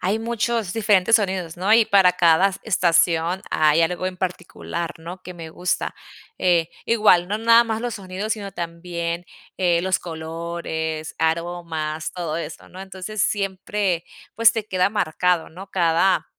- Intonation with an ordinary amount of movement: Yes, average, 3.0 semitones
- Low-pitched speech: No, medium, 180 Hz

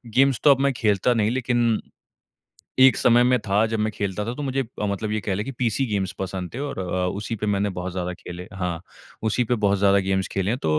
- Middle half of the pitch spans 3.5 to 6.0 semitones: Yes, average, 4.1 semitones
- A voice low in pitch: Yes, low, 105 Hz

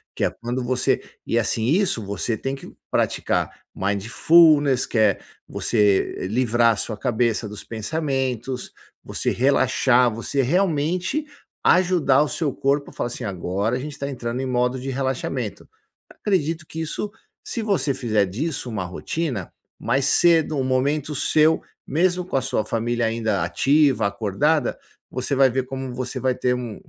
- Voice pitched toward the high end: No, low, 130 Hz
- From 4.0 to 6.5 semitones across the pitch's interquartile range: Yes, average, 4.4 semitones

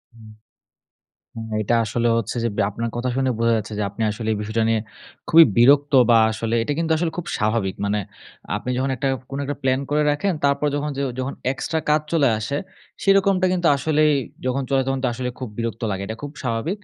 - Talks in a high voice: No, low, 130 Hz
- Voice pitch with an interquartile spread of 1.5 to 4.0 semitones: No, average, 4.5 semitones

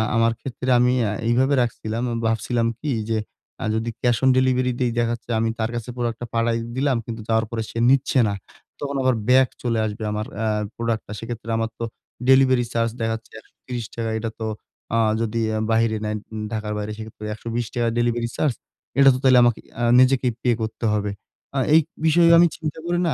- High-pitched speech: No, low, 115 Hz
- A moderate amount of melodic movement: No, narrow, 2.3 semitones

